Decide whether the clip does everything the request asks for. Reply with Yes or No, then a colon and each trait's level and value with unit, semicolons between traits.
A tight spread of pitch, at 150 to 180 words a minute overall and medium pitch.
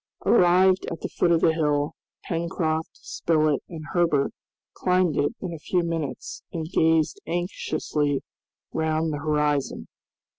No: narrow, 2.3 semitones; slow, 135 wpm; medium, 160 Hz